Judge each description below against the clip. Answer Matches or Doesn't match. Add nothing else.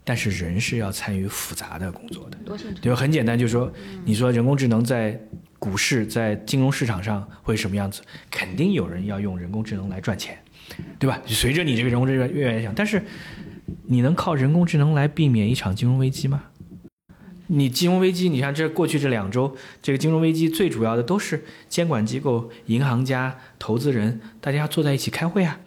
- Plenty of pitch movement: Matches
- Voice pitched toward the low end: Matches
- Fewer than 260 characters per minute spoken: Doesn't match